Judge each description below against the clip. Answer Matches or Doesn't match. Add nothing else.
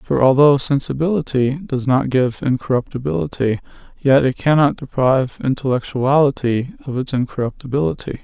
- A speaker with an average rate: Doesn't match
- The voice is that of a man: Matches